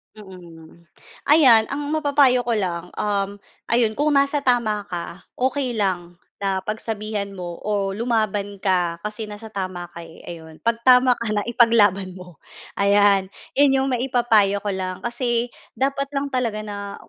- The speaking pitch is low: No, high, 210 Hz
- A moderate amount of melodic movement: Yes, average, 4.3 semitones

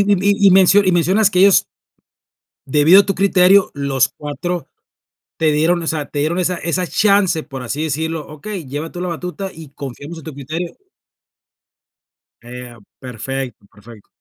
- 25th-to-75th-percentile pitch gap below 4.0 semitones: No, average, 4.5 semitones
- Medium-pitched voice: Yes, medium, 160 Hz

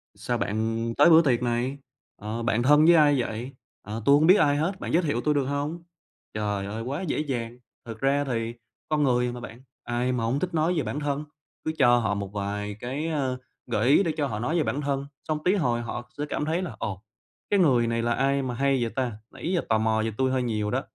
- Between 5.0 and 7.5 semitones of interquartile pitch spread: No, average, 4.4 semitones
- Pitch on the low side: Yes, low, 130 Hz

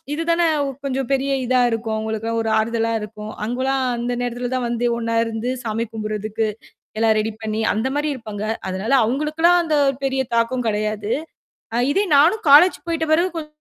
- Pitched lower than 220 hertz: No, high, 235 Hz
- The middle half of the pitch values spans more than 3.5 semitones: Yes, average, 3.9 semitones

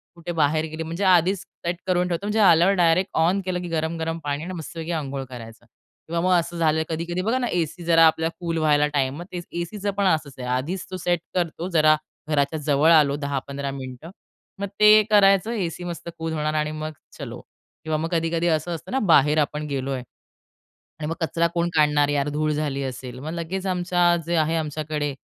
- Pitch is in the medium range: Yes, medium, 160 Hz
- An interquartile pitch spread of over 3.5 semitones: No, average, 2.8 semitones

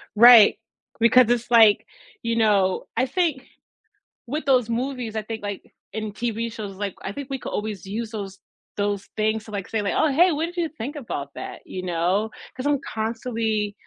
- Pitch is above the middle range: Yes, high, 225 Hz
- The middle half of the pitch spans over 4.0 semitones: No, average, 3.5 semitones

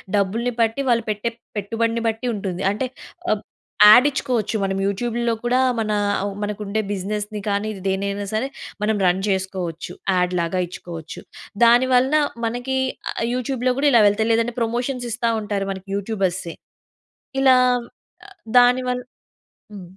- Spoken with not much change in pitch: No, average, 3.6 semitones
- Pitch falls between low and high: No, high, 215 Hz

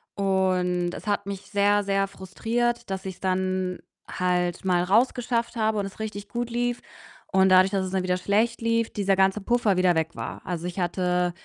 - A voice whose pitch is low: No, high, 195 Hz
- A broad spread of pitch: No, average, 2.8 semitones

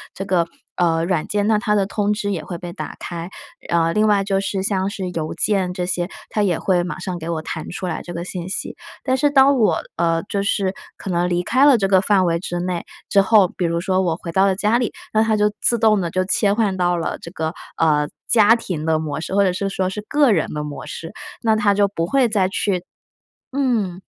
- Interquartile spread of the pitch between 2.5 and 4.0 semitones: Yes, average, 3.2 semitones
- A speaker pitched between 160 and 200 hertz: Yes, high, 190 Hz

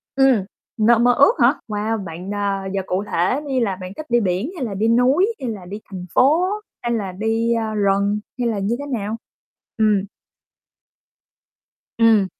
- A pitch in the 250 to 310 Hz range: No, high, 220 Hz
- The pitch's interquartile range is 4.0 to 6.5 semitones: No, average, 3.4 semitones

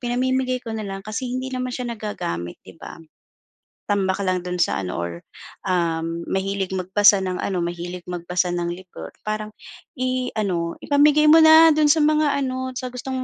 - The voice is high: Yes, high, 205 Hz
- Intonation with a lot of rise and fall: Yes, wide, 6.2 semitones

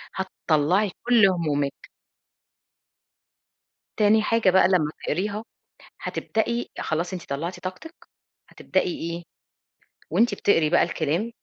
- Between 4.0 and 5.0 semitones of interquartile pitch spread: Yes, average, 4.4 semitones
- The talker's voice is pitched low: No, medium, 185 Hz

